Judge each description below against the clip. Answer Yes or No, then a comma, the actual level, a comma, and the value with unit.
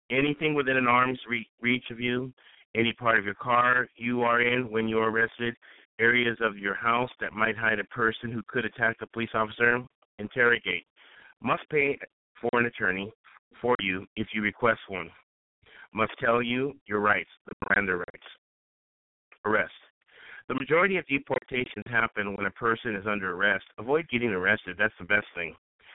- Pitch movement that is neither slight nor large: No, narrow, 1.9 semitones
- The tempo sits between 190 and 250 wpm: No, average, 170 wpm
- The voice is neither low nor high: No, low, 115 Hz